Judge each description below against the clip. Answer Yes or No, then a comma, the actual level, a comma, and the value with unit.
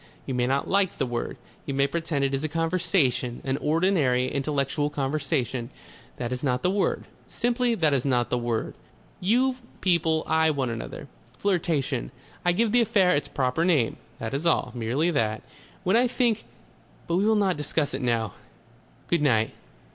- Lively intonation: Yes, wide, 6.0 semitones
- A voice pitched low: No, medium, 150 Hz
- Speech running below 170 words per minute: No, average, 175 wpm